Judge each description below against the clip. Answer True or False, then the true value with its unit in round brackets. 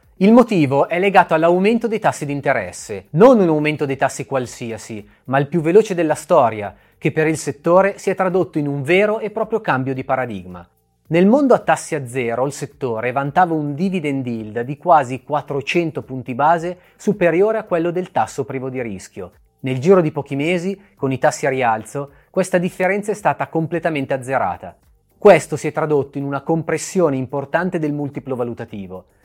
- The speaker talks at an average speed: False (180 wpm)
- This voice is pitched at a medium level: True (150 Hz)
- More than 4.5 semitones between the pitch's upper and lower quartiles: True (4.9 semitones)